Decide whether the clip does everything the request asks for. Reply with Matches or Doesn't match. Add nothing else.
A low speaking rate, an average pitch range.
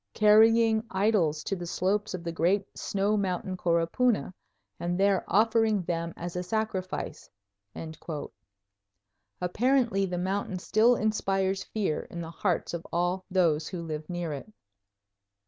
Matches